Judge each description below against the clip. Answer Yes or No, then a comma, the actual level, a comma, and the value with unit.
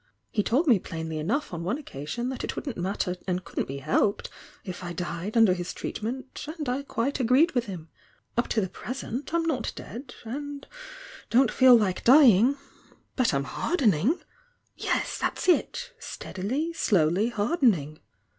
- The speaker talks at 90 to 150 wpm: No, average, 165 wpm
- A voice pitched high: Yes, high, 230 Hz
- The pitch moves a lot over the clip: Yes, wide, 7.0 semitones